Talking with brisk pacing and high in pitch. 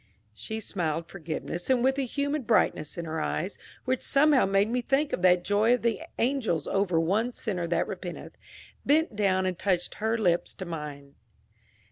No: average, 175 wpm; high, 200 Hz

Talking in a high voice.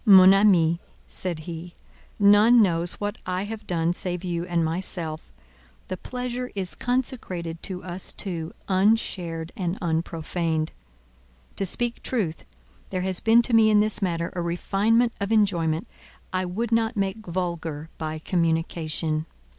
No: medium, 180 Hz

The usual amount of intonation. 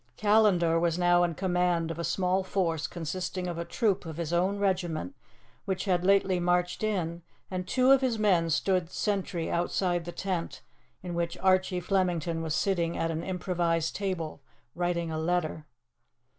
No: narrow, 2.1 semitones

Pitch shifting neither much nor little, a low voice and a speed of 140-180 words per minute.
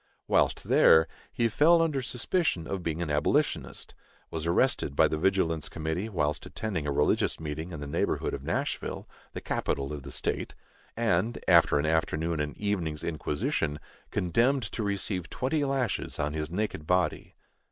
No: wide, 6.2 semitones; very low, 85 Hz; average, 160 wpm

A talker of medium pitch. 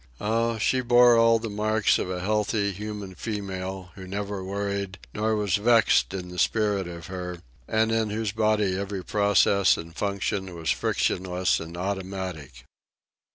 No: low, 100 Hz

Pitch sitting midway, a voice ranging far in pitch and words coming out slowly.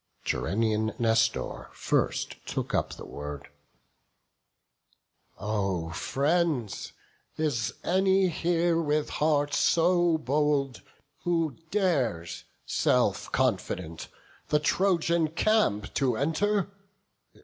Yes: medium, 150 Hz; wide, 7.3 semitones; slow, 85 wpm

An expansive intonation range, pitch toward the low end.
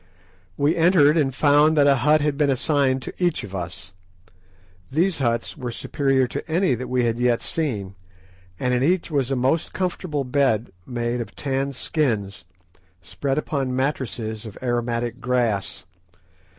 No: average, 3.8 semitones; low, 130 Hz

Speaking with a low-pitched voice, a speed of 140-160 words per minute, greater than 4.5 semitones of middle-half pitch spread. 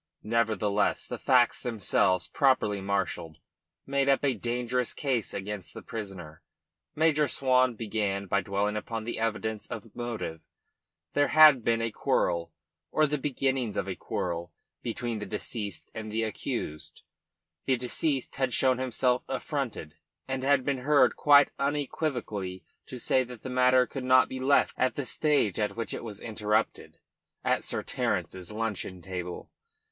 No: low, 115 Hz; average, 150 wpm; average, 4.2 semitones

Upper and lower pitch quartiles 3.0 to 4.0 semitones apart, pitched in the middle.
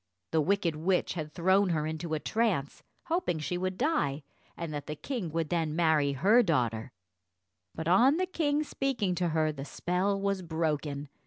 No: average, 4.6 semitones; medium, 170 Hz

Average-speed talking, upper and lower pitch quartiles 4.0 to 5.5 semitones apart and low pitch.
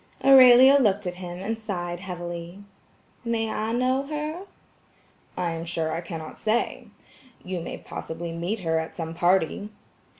No: average, 145 wpm; average, 5.0 semitones; medium, 185 Hz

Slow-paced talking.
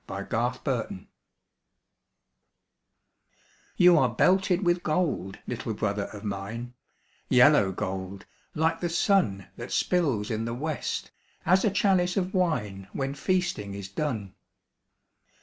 Yes: slow, 120 wpm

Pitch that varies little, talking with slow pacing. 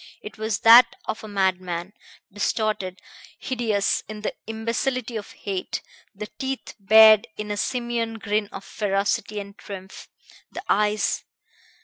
Yes: narrow, 2.1 semitones; slow, 130 wpm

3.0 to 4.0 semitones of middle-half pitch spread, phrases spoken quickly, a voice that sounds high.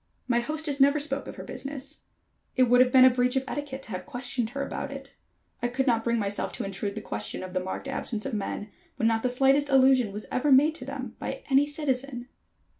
Yes: average, 3.3 semitones; fast, 230 wpm; very high, 255 Hz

